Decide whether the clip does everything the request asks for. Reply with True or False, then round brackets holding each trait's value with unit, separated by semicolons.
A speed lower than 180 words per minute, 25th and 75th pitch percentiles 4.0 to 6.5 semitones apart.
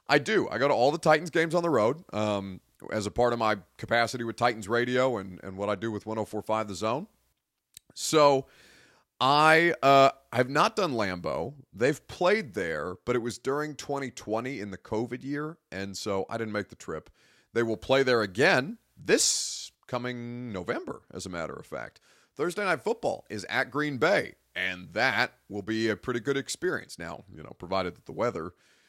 False (190 wpm; 4.3 semitones)